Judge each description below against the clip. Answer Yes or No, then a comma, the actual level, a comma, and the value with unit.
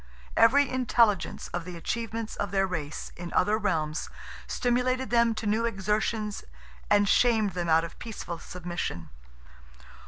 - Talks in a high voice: Yes, high, 210 Hz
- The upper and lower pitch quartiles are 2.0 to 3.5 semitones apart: No, average, 4.8 semitones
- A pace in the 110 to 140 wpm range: Yes, slow, 135 wpm